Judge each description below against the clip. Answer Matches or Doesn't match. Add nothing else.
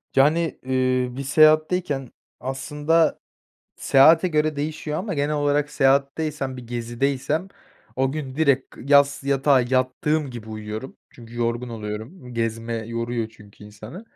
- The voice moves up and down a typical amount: Matches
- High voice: Doesn't match